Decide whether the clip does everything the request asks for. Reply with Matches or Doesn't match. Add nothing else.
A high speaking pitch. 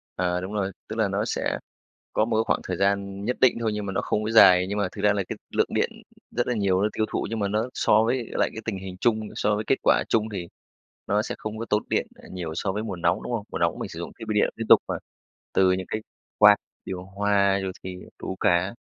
Doesn't match